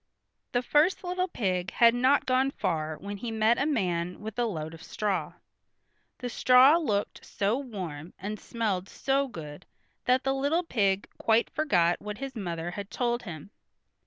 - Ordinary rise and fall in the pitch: No, wide, 6.2 semitones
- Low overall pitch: No, high, 220 Hz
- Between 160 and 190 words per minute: Yes, average, 165 wpm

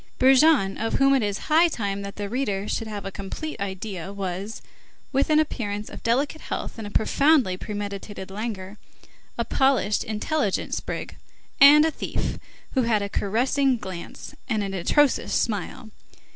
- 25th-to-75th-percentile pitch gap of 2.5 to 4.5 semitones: No, average, 5.3 semitones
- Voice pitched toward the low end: No, high, 215 Hz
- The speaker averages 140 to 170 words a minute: Yes, average, 160 wpm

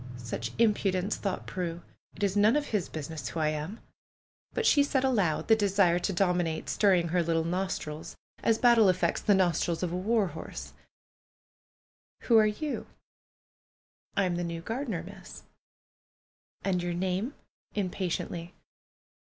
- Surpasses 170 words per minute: No, average, 155 wpm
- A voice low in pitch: No, medium, 185 Hz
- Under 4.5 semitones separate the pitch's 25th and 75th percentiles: Yes, average, 3.9 semitones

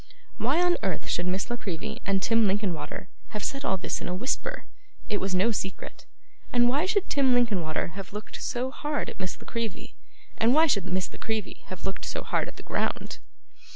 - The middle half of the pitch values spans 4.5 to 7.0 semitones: Yes, average, 4.9 semitones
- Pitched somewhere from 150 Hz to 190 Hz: No, high, 215 Hz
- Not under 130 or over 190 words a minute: No, fast, 205 wpm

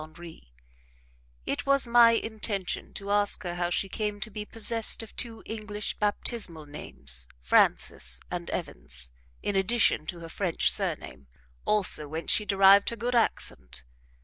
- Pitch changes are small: No, wide, 5.4 semitones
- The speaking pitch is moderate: No, high, 195 Hz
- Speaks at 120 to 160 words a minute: Yes, average, 150 wpm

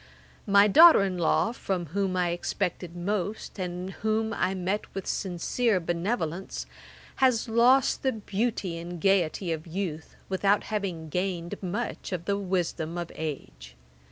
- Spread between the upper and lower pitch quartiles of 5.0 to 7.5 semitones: No, average, 3.2 semitones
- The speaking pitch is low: No, medium, 185 Hz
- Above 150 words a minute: No, average, 140 wpm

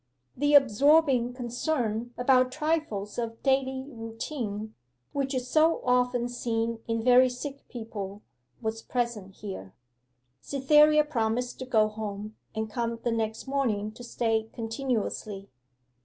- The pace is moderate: No, slow, 125 wpm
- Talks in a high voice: Yes, high, 240 Hz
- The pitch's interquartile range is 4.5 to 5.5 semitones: No, average, 3.2 semitones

